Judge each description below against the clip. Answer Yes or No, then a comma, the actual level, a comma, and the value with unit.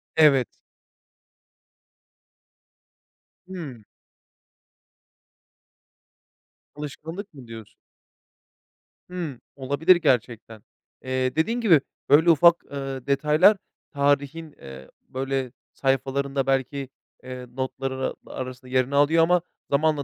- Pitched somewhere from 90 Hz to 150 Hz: Yes, medium, 140 Hz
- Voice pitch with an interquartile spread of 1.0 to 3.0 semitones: No, average, 3.4 semitones